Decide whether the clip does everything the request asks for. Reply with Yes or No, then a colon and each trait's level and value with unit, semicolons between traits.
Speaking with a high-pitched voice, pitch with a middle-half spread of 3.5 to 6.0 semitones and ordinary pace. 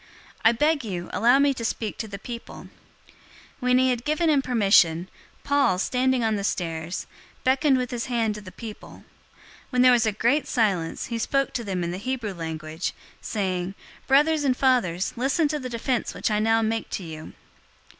Yes: high, 230 Hz; average, 5.1 semitones; average, 195 wpm